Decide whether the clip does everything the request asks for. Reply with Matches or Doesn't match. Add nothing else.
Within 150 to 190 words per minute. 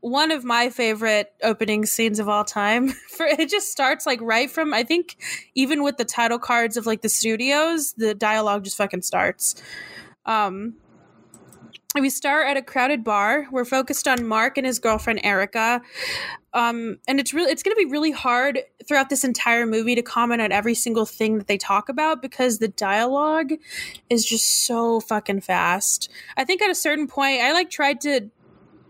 Matches